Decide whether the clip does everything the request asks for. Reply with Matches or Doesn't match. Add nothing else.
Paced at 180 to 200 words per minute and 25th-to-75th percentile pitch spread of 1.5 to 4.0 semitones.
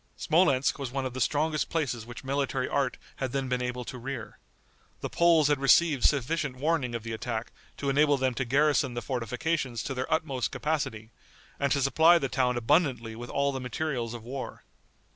Matches